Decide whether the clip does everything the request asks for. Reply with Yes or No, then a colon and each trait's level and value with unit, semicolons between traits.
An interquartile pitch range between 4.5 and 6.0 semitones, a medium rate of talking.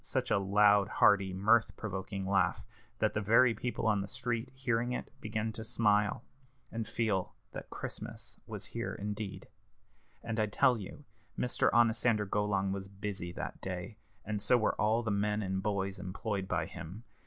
No: narrow, 2.6 semitones; average, 165 wpm